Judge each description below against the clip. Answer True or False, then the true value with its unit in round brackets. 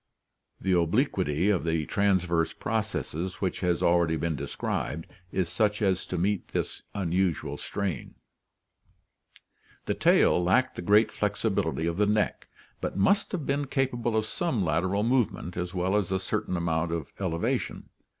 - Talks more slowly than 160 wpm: True (150 wpm)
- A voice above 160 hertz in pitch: False (95 Hz)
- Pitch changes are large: False (3.7 semitones)